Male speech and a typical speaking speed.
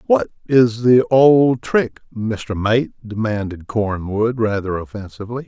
No: male; slow, 120 wpm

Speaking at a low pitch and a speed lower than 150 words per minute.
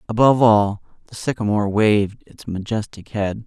Yes: low, 105 Hz; average, 140 wpm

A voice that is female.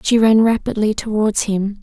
Yes: female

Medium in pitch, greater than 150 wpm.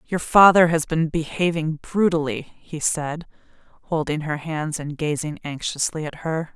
No: medium, 160 Hz; average, 145 wpm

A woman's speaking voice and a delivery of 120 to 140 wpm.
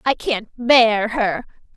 Yes: female; slow, 135 wpm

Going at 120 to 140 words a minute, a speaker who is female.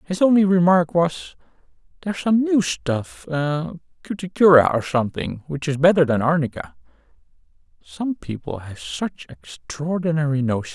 No: slow, 135 wpm; male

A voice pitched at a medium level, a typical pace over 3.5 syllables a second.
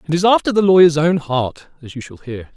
Yes: medium, 160 Hz; 5.8 syllables/s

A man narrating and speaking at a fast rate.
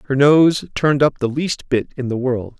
Yes: male; fast, 230 wpm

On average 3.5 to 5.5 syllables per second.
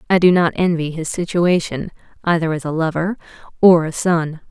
Yes: 5.2 syllables/s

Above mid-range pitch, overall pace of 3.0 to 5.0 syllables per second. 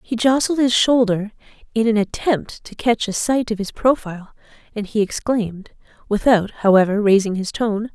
Yes: high, 220 Hz; 4.9 syllables/s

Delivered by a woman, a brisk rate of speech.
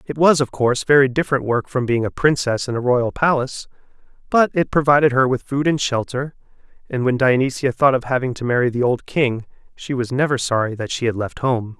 No: male; fast, 220 wpm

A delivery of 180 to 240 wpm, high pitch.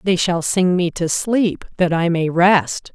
No: fast, 205 wpm; medium, 175 Hz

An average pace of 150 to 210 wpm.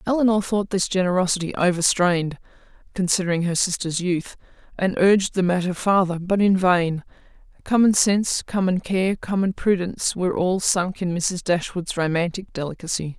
No: average, 140 wpm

